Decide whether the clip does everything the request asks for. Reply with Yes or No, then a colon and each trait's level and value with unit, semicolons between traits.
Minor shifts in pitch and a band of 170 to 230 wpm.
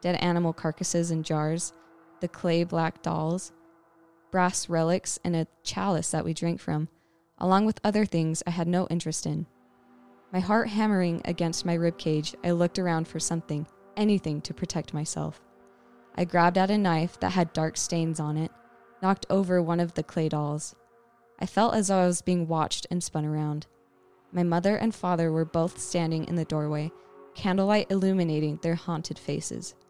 Yes: narrow, 2.2 semitones; average, 175 wpm